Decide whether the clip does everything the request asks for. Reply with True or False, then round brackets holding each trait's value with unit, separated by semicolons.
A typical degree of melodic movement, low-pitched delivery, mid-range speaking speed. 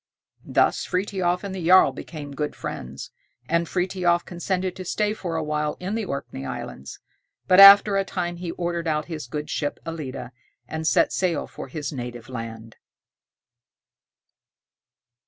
False (4.1 semitones; 170 Hz; 150 wpm)